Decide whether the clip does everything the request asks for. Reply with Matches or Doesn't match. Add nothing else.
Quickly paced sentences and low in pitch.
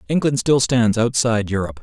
Doesn't match